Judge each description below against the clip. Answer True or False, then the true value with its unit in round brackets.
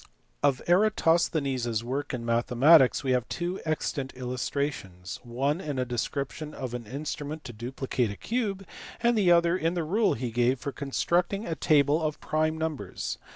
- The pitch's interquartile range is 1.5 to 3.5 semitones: False (4.8 semitones)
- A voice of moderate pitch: True (145 Hz)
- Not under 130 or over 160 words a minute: False (170 wpm)